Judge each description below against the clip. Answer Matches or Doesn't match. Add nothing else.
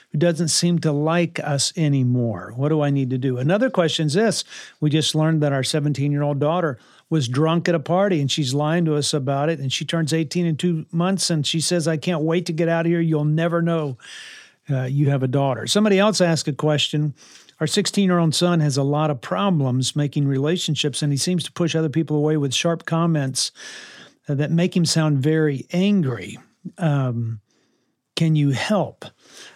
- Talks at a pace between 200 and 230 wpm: Matches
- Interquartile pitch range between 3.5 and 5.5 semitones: Doesn't match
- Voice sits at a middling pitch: Matches